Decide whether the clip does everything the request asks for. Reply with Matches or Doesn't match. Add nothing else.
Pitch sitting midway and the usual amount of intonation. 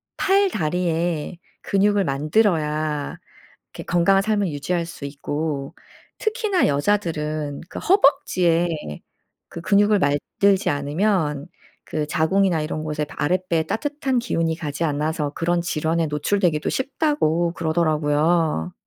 Matches